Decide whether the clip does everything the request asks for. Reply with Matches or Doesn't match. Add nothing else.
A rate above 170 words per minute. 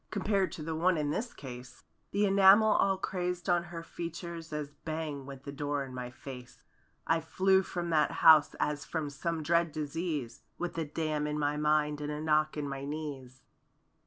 Matches